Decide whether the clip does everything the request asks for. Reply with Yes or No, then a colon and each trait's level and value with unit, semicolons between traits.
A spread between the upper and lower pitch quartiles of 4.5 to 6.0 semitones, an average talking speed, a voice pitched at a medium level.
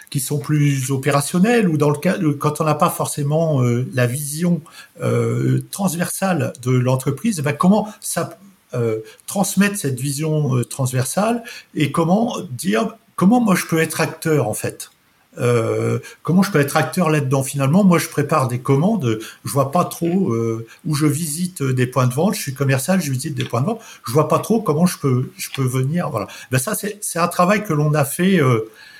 Yes: average, 5.1 semitones; average, 200 wpm; medium, 150 Hz